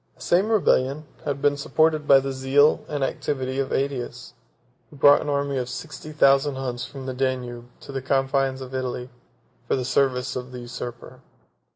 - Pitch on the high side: No, low, 135 Hz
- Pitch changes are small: Yes, narrow, 1.9 semitones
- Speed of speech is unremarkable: Yes, average, 180 wpm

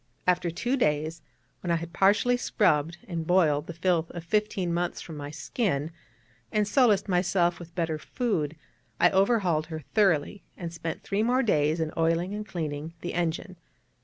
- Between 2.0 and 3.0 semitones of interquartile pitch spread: No, average, 3.6 semitones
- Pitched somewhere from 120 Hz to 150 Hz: No, medium, 175 Hz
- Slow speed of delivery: No, average, 165 wpm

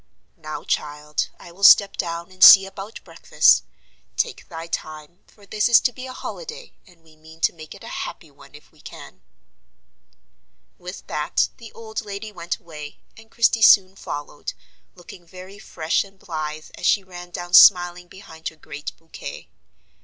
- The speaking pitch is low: No, medium, 175 Hz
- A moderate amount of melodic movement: Yes, average, 3.9 semitones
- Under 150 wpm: No, average, 170 wpm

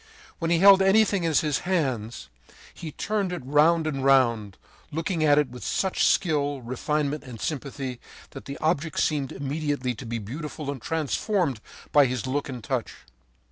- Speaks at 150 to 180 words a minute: Yes, average, 165 wpm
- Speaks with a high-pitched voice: No, medium, 145 Hz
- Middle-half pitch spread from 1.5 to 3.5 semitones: No, average, 4.0 semitones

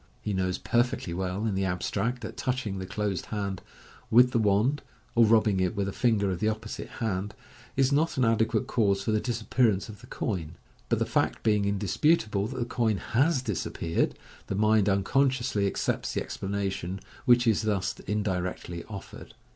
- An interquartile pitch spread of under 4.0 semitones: Yes, average, 3.3 semitones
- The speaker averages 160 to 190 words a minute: Yes, average, 175 wpm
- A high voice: No, low, 105 Hz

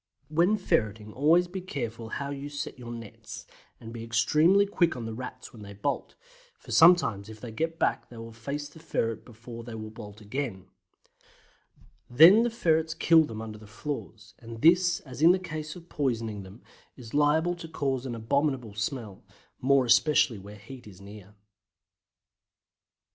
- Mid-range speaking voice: No, low, 125 Hz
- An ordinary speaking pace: Yes, average, 170 wpm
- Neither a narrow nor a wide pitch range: No, wide, 6.0 semitones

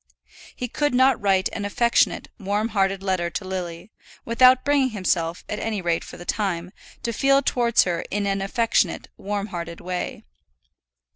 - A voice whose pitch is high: Yes, high, 200 Hz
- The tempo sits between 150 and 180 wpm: Yes, average, 160 wpm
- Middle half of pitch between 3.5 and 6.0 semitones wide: Yes, average, 4.3 semitones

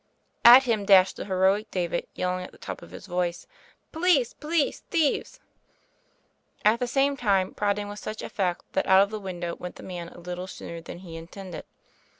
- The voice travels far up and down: No, average, 4.3 semitones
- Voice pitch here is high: Yes, high, 195 Hz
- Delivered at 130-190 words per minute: No, average, 200 wpm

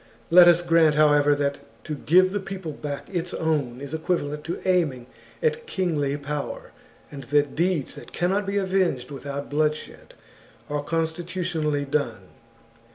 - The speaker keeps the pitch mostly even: No, average, 3.6 semitones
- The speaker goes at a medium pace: Yes, average, 145 wpm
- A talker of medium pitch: Yes, medium, 155 Hz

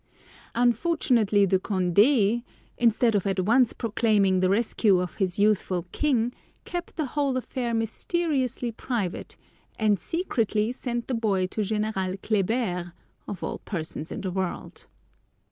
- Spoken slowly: Yes, slow, 130 wpm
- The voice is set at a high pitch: Yes, high, 215 Hz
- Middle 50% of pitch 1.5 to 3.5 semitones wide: No, average, 4.2 semitones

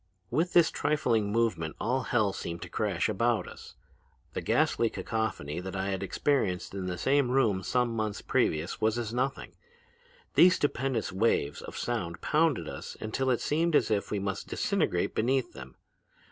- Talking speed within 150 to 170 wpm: Yes, average, 165 wpm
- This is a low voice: Yes, low, 110 Hz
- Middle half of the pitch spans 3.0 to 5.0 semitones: No, wide, 5.6 semitones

